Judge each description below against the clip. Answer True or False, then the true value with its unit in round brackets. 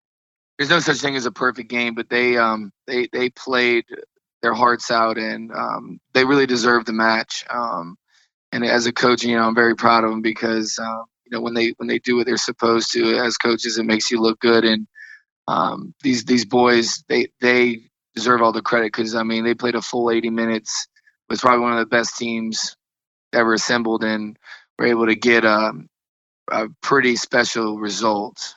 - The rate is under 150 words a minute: False (200 wpm)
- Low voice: True (115 Hz)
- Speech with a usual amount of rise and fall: False (1.5 semitones)